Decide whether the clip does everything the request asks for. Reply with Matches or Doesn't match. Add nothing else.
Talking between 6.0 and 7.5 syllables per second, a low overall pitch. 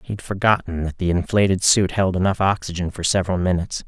Matches